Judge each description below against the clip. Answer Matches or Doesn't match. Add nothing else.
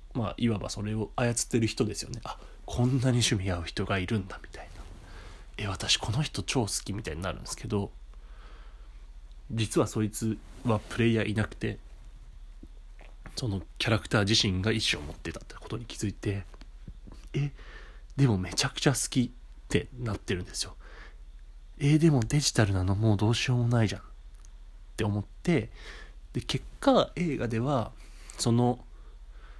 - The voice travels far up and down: Doesn't match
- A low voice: Matches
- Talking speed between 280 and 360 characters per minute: Matches